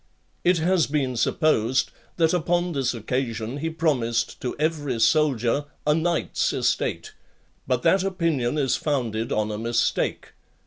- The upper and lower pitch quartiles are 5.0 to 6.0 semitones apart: Yes, wide, 5.5 semitones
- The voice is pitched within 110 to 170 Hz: Yes, medium, 140 Hz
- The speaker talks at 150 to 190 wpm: No, slow, 135 wpm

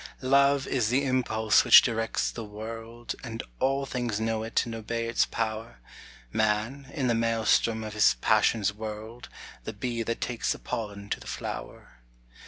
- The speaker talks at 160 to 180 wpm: Yes, average, 165 wpm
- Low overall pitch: Yes, low, 115 Hz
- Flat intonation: Yes, narrow, 1.7 semitones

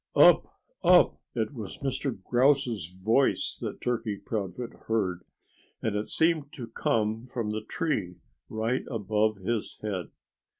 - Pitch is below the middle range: Yes, low, 110 Hz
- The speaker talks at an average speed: No, slow, 130 wpm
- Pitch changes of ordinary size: Yes, average, 3.4 semitones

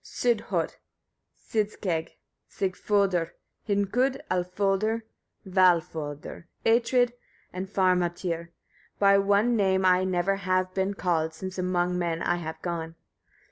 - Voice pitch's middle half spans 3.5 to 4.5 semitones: No, narrow, 2.4 semitones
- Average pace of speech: No, slow, 100 wpm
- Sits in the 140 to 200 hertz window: Yes, medium, 185 Hz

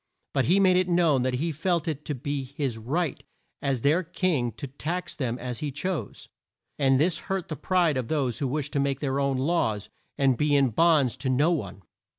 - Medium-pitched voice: Yes, medium, 145 Hz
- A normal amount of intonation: Yes, average, 4.2 semitones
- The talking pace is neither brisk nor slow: No, fast, 210 wpm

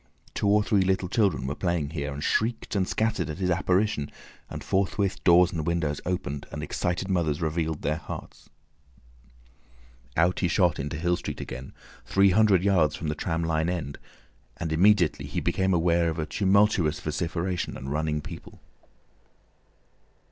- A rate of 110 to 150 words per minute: No, average, 160 wpm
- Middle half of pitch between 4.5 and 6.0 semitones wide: No, average, 3.5 semitones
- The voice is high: No, very low, 85 Hz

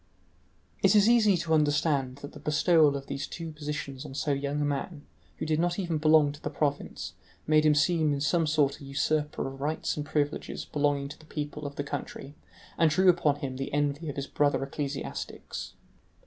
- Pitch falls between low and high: Yes, medium, 150 Hz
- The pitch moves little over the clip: Yes, narrow, 1.7 semitones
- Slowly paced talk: No, average, 200 wpm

